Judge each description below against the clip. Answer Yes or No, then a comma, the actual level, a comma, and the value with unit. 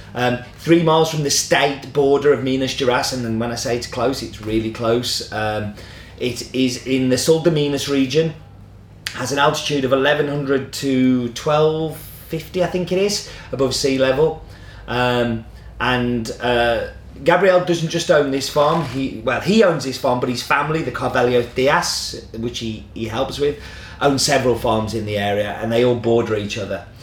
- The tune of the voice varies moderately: Yes, average, 3.9 semitones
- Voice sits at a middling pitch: No, low, 125 Hz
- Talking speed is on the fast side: No, average, 180 wpm